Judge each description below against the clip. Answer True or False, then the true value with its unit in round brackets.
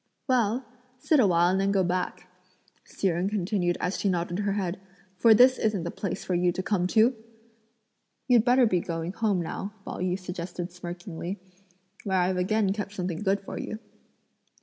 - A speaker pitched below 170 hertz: False (190 Hz)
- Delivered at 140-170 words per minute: False (180 wpm)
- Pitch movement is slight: False (3.0 semitones)